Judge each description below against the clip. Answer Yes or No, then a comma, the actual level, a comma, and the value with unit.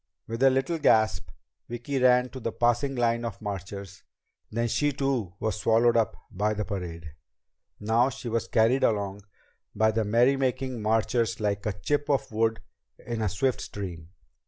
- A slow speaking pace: No, average, 165 wpm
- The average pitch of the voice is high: No, low, 115 Hz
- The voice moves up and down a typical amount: Yes, average, 3.4 semitones